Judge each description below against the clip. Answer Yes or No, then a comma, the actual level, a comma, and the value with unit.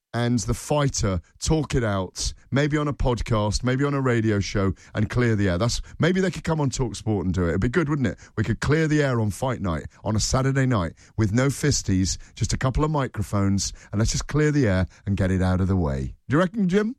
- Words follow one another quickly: Yes, fast, 255 wpm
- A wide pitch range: Yes, wide, 6.3 semitones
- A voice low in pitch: Yes, low, 115 Hz